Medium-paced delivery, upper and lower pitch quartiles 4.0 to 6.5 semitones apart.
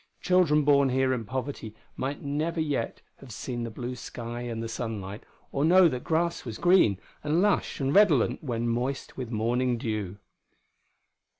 Yes: average, 165 wpm; average, 4.3 semitones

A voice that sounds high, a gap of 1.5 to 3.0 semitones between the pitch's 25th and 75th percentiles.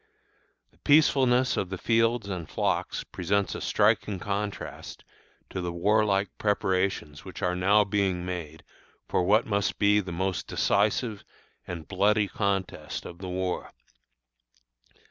No: low, 100 Hz; narrow, 2.5 semitones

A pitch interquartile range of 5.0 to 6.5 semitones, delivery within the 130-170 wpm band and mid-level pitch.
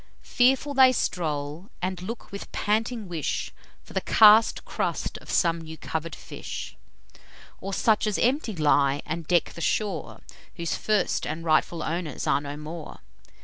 Yes: average, 5.3 semitones; average, 150 wpm; medium, 175 Hz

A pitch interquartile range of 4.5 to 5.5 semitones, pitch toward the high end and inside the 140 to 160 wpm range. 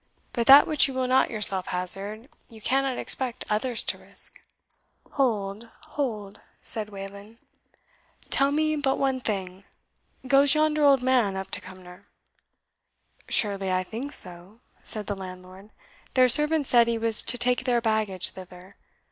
Yes: average, 5.1 semitones; high, 225 Hz; average, 150 wpm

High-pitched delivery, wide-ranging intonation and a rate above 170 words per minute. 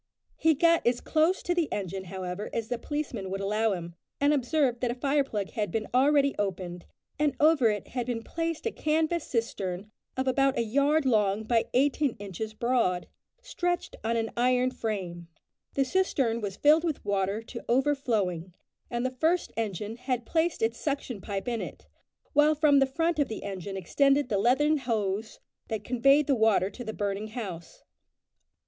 Yes: high, 240 Hz; wide, 5.8 semitones; average, 180 wpm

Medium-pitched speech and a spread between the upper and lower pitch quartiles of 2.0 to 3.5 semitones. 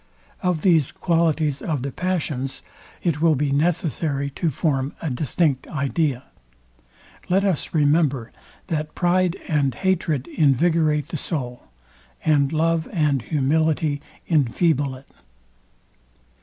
Yes: medium, 155 Hz; average, 3.1 semitones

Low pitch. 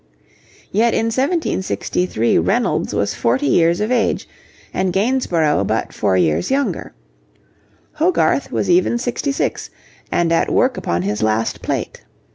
No: medium, 185 Hz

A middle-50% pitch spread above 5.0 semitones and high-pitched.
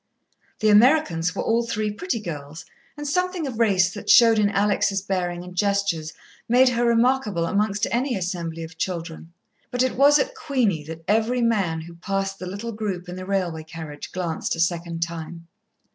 Yes: wide, 5.5 semitones; high, 195 Hz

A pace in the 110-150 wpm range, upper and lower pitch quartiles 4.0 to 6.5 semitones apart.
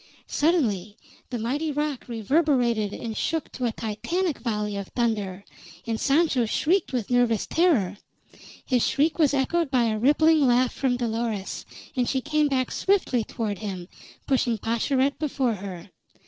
Yes: average, 145 wpm; average, 5.0 semitones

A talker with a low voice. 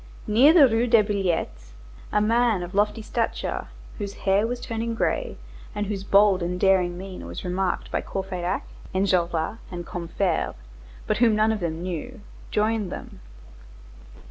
No: high, 200 Hz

